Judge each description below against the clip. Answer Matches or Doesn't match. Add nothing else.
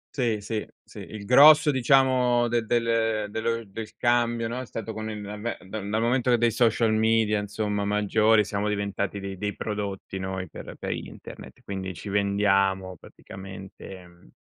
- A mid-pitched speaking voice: Doesn't match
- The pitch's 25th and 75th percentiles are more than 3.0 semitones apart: Doesn't match